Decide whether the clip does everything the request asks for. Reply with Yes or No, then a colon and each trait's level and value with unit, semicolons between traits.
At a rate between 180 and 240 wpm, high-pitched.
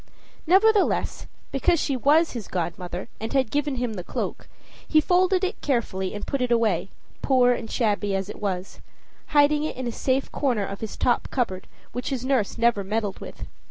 Yes: average, 185 wpm; high, 245 Hz